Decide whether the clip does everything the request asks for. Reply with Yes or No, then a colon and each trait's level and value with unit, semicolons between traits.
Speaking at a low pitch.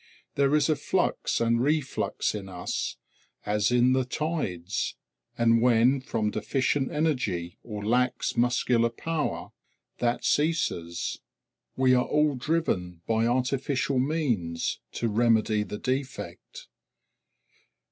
Yes: low, 125 Hz